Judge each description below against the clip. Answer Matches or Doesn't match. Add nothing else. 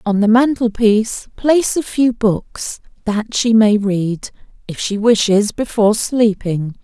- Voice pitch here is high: Matches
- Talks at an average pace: Matches